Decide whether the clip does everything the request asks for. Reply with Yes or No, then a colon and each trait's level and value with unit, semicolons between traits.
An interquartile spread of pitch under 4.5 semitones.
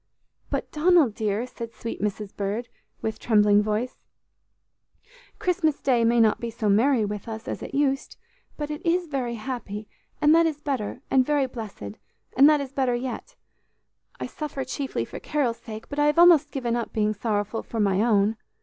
No: average, 5.0 semitones